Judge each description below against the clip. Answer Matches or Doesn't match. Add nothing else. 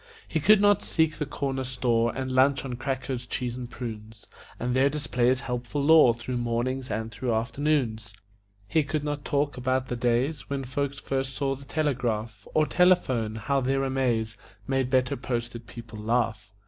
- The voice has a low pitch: Matches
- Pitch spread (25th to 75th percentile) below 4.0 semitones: Matches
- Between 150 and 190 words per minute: Matches